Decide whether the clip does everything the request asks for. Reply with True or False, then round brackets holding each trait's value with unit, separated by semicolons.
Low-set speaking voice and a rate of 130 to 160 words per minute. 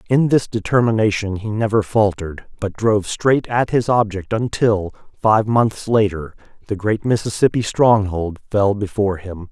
True (105 Hz; 145 wpm)